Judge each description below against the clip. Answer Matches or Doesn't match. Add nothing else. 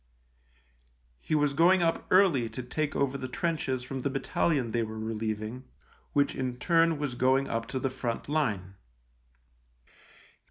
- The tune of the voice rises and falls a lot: Doesn't match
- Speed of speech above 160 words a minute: Doesn't match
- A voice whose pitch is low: Matches